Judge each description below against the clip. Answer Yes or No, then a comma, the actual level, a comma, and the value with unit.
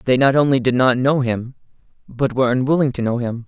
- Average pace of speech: No, fast, 225 wpm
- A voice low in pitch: Yes, low, 130 Hz